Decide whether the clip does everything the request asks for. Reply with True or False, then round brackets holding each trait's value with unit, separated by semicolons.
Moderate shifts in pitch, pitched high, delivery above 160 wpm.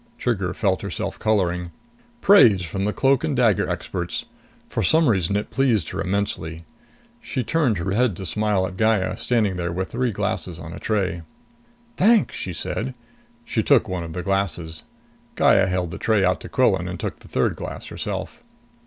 False (4.0 semitones; 100 Hz; 180 wpm)